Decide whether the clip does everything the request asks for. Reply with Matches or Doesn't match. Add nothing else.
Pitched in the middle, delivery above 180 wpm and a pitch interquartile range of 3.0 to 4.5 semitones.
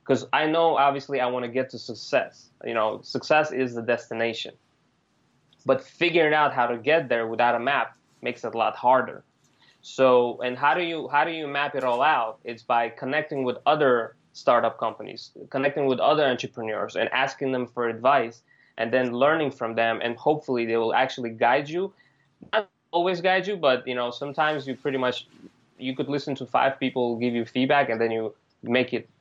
Doesn't match